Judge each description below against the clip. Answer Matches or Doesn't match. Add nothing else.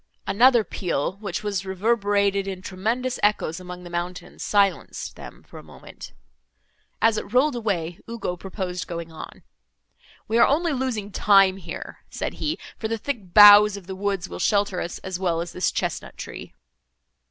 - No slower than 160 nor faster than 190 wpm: Matches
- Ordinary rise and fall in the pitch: Matches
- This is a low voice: Doesn't match